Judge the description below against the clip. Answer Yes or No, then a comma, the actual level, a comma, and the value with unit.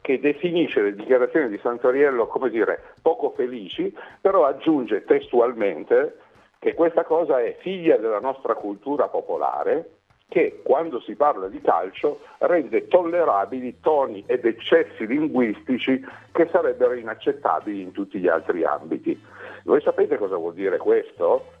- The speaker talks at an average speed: Yes, average, 135 wpm